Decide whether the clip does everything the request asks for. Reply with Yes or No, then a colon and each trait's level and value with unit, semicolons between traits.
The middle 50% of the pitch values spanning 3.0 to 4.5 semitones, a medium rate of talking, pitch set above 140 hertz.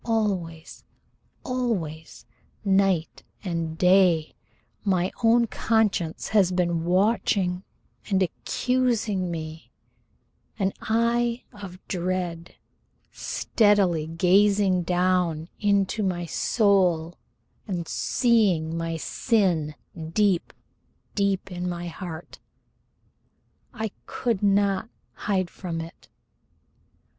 No: average, 3.3 semitones; slow, 85 wpm; medium, 185 Hz